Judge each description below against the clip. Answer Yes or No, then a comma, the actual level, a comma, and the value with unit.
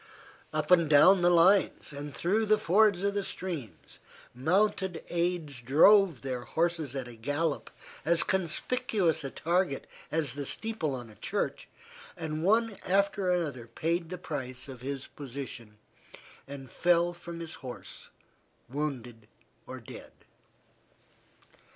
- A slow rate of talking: Yes, slow, 130 wpm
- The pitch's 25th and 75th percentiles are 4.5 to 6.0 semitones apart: Yes, average, 5.1 semitones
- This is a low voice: No, medium, 165 Hz